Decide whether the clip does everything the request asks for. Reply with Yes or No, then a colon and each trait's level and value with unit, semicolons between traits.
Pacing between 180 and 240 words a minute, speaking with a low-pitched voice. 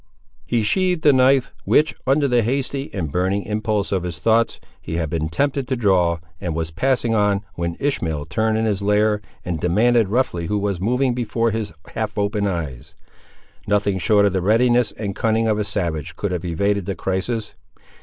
Yes: average, 185 wpm; low, 105 Hz